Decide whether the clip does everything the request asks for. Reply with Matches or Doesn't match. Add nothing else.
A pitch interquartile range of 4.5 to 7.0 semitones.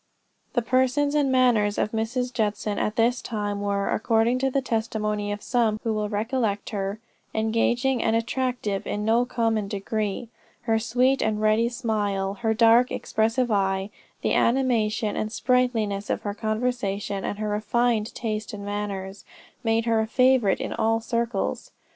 Doesn't match